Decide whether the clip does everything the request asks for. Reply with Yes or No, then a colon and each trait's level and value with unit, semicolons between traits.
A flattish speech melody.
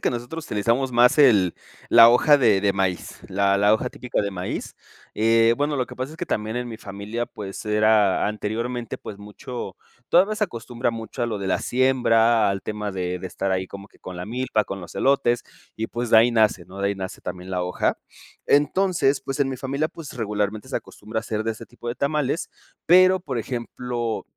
No: average, 4.0 semitones